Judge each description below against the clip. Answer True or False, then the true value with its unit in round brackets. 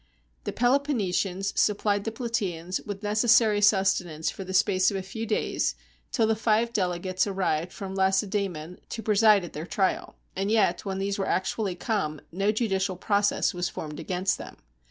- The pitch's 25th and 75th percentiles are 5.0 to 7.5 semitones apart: False (2.5 semitones)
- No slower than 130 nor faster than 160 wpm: False (170 wpm)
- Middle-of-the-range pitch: False (195 Hz)